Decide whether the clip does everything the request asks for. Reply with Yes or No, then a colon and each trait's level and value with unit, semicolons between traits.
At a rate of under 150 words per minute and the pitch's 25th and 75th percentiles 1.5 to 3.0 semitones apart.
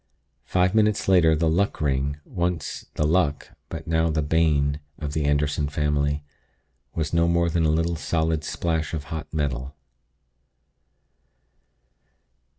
Yes: slow, 135 wpm; narrow, 2.4 semitones